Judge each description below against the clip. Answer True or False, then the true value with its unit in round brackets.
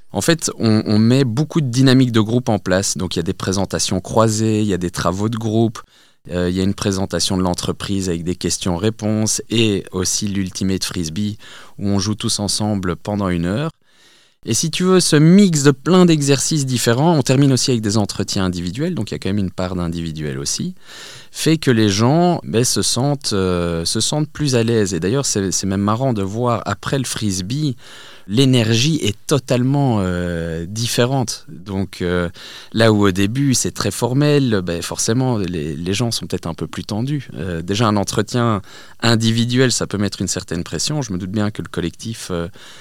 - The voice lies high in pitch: False (105 Hz)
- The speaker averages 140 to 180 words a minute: False (200 wpm)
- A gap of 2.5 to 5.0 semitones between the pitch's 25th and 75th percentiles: False (5.4 semitones)